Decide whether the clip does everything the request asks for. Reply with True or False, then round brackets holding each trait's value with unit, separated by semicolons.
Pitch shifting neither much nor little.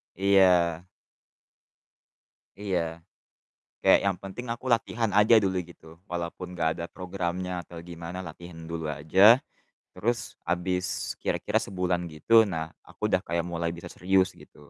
False (2.2 semitones)